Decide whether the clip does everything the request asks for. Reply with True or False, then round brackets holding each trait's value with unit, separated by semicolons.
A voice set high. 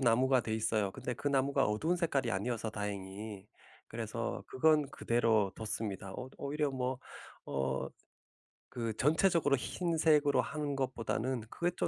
False (125 Hz)